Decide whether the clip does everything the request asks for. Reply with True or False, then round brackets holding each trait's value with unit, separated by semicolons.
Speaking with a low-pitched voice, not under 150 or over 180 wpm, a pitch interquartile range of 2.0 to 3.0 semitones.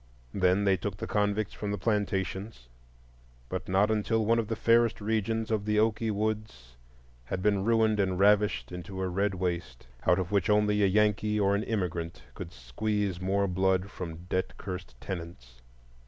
True (100 Hz; 170 wpm; 2.6 semitones)